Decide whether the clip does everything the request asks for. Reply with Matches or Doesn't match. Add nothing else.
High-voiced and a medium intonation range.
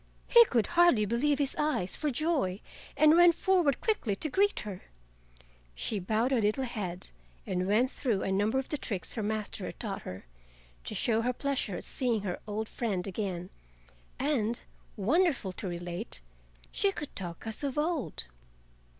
Doesn't match